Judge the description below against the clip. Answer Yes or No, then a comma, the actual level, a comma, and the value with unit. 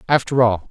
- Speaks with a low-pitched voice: Yes, low, 120 Hz